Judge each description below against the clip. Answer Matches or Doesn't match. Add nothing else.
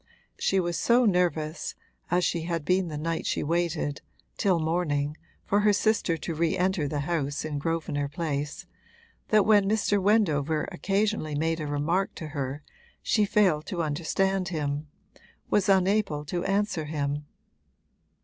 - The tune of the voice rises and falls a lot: Doesn't match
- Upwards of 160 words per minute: Doesn't match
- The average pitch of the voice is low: Doesn't match